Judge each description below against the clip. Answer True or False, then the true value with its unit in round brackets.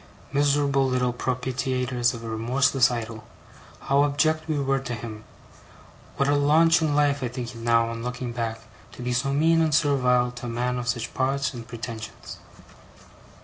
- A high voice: False (125 Hz)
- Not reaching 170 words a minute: False (175 wpm)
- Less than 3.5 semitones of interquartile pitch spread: True (2.8 semitones)